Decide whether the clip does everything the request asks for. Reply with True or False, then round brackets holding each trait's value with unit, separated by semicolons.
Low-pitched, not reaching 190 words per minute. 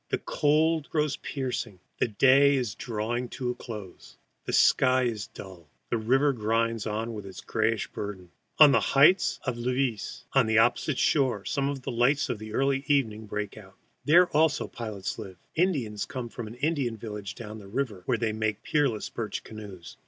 True (120 Hz; 165 wpm)